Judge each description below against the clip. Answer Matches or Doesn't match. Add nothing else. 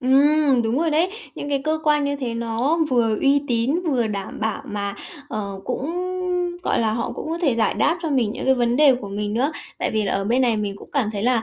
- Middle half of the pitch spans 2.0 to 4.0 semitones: Doesn't match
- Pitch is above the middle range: Matches